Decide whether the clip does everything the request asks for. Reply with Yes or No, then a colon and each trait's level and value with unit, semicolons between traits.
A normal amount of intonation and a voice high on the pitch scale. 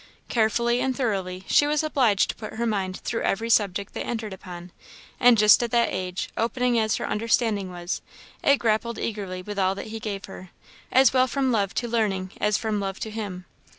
Yes: average, 3.5 semitones; high, 215 Hz